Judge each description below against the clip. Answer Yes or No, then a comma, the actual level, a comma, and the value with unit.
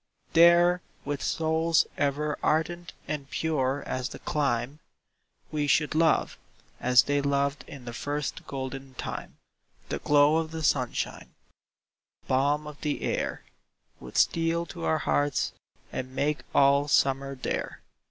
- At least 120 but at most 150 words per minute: Yes, slow, 135 wpm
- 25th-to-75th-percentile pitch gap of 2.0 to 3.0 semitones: Yes, narrow, 2.6 semitones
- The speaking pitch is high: No, medium, 145 Hz